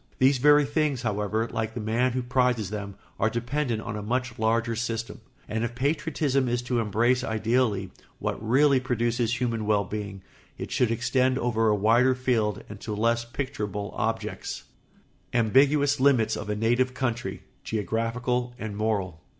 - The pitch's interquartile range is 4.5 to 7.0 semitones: No, average, 2.8 semitones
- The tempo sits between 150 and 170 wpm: Yes, average, 160 wpm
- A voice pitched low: Yes, low, 115 Hz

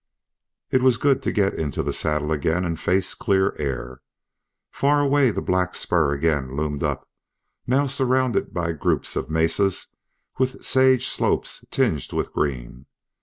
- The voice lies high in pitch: No, very low, 90 Hz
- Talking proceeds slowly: No, average, 150 wpm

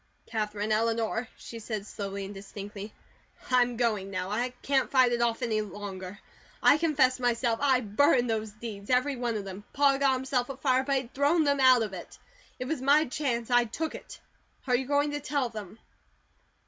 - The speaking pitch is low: No, high, 240 Hz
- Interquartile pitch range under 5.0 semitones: Yes, average, 3.8 semitones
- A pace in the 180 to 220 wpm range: Yes, average, 185 wpm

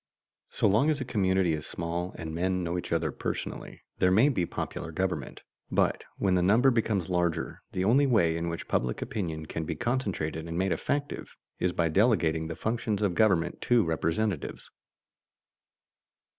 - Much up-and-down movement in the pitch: No, average, 4.7 semitones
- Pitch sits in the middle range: No, very low, 90 Hz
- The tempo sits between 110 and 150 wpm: No, average, 170 wpm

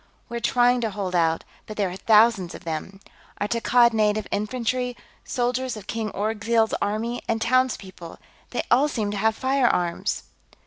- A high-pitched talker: Yes, high, 220 Hz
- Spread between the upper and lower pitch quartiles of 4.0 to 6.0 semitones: No, average, 3.2 semitones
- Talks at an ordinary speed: Yes, average, 160 wpm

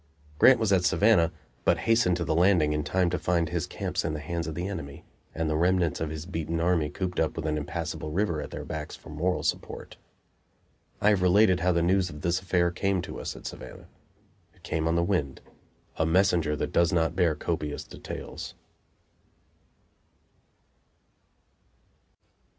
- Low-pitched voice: Yes, very low, 85 Hz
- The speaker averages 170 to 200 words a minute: Yes, average, 180 wpm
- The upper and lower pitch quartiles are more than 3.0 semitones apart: No, narrow, 2.6 semitones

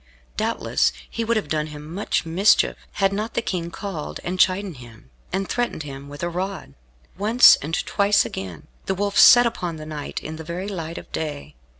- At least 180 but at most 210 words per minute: Yes, average, 195 wpm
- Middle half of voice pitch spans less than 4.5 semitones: No, average, 4.8 semitones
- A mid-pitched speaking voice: Yes, medium, 175 Hz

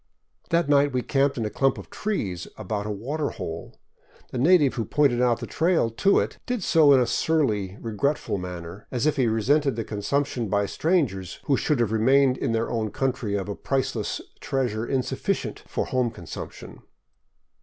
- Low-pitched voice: Yes, low, 125 Hz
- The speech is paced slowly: No, average, 185 wpm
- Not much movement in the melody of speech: No, average, 4.8 semitones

